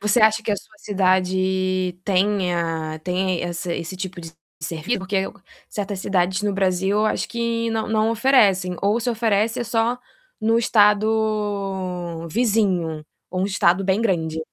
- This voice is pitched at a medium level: No, high, 195 Hz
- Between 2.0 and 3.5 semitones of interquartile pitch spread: Yes, average, 3.0 semitones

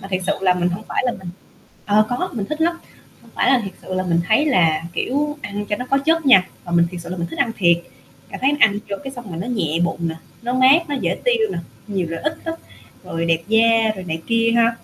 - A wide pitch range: Yes, wide, 6.6 semitones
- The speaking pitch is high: Yes, high, 215 Hz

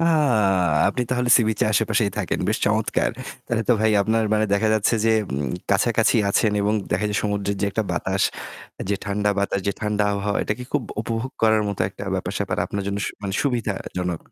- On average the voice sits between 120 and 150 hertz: No, low, 105 Hz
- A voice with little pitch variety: Yes, narrow, 2.0 semitones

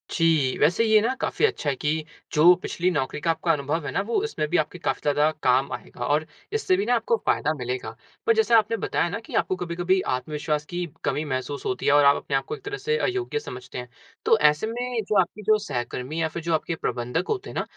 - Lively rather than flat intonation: Yes, wide, 7.2 semitones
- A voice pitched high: No, medium, 165 Hz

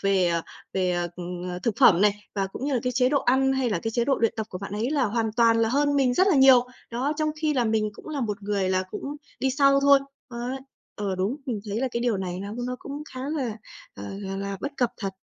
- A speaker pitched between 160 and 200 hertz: No, high, 235 Hz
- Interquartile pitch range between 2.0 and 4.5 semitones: No, average, 5.0 semitones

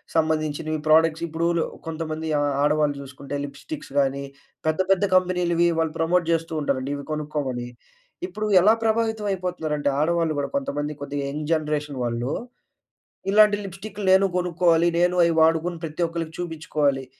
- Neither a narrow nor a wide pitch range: Yes, average, 3.1 semitones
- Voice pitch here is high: No, medium, 160 Hz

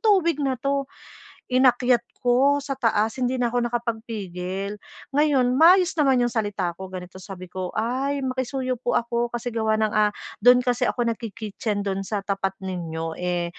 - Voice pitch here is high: Yes, high, 235 Hz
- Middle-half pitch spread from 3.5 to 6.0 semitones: Yes, average, 4.5 semitones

